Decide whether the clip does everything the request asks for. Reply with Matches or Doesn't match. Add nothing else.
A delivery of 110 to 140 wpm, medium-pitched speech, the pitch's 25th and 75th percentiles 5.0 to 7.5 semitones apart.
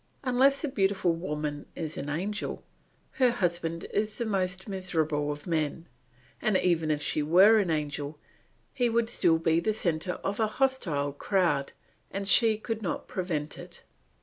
Doesn't match